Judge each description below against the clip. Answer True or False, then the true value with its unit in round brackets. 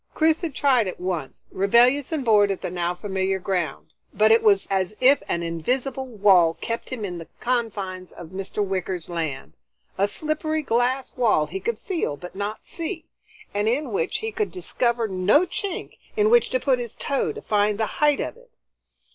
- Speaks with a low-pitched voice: False (215 Hz)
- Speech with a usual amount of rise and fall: False (6.7 semitones)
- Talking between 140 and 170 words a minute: False (190 wpm)